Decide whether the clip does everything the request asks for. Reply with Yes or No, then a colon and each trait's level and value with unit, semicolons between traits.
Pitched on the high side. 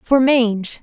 Yes: high, 240 Hz